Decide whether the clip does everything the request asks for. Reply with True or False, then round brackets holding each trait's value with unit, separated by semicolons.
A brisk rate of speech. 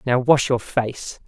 False (190 wpm)